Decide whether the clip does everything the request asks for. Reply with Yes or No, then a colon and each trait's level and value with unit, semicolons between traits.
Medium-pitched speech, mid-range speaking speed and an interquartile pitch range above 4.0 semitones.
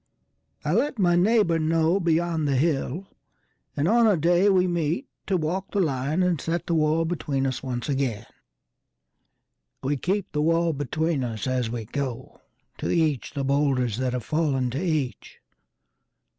Yes: medium, 155 Hz; average, 145 wpm; average, 4.7 semitones